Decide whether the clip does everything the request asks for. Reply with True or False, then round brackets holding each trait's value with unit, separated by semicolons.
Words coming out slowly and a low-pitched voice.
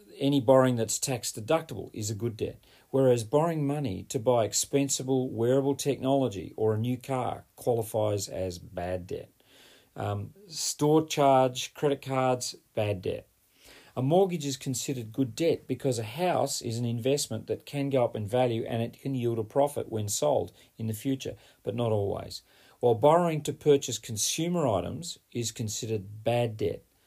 False (165 wpm; 125 Hz)